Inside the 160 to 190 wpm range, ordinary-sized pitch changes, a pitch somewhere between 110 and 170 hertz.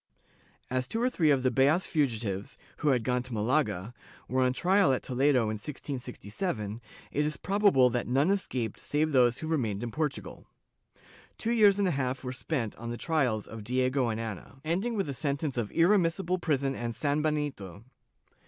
Yes: average, 180 wpm; average, 4.8 semitones; low, 135 Hz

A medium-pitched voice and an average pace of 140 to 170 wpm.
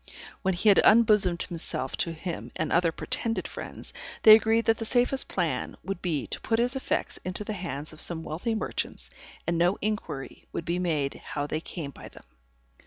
No: medium, 180 Hz; average, 190 wpm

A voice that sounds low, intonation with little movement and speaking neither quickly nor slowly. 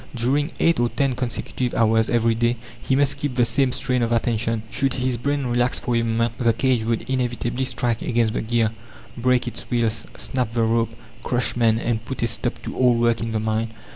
No: low, 120 Hz; narrow, 1.8 semitones; fast, 210 wpm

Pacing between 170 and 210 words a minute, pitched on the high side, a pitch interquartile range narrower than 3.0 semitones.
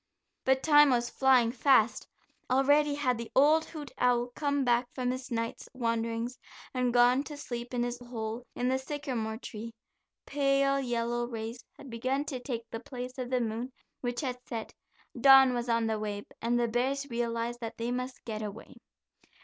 Yes: average, 175 wpm; high, 245 Hz; narrow, 2.4 semitones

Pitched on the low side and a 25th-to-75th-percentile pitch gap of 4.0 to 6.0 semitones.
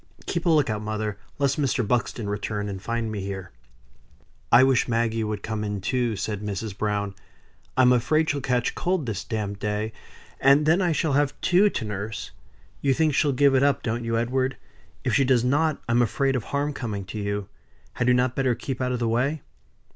Yes: low, 120 Hz; average, 4.4 semitones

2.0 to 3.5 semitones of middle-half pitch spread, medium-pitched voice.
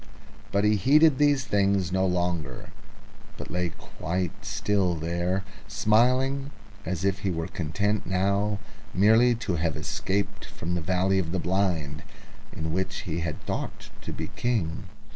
No: average, 3.2 semitones; very low, 95 Hz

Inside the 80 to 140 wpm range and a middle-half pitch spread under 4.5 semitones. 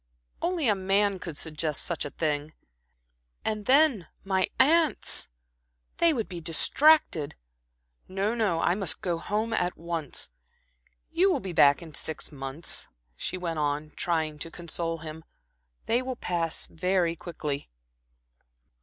No: slow, 135 wpm; average, 5.1 semitones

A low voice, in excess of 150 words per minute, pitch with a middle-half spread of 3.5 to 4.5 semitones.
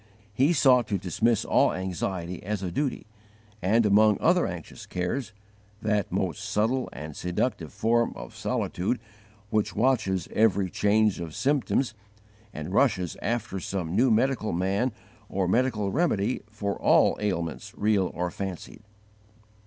No: low, 105 Hz; slow, 135 wpm; average, 4.2 semitones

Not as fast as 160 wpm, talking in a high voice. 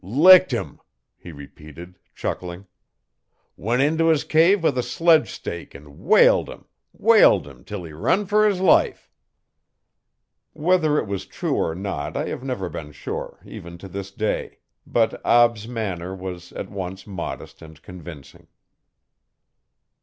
No: average, 145 wpm; low, 100 Hz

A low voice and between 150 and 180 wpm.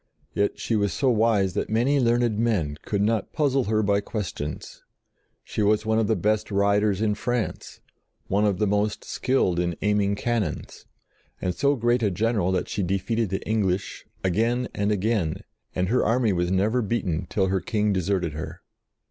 Yes: low, 105 Hz; average, 175 wpm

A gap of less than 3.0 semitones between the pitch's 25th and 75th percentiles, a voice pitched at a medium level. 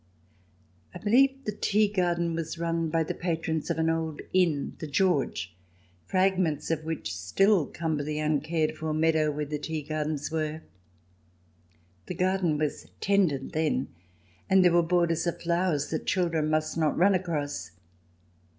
Yes: narrow, 2.6 semitones; medium, 160 Hz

